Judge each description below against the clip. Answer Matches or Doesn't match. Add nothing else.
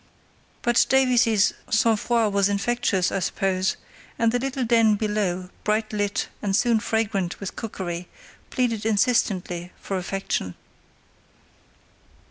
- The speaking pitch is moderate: Doesn't match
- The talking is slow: Matches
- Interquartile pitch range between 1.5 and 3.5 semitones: Matches